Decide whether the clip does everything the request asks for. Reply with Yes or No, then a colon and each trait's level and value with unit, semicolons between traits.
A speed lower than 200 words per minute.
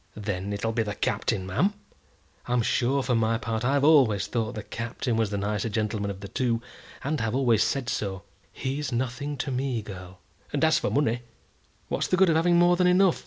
No: fast, 205 wpm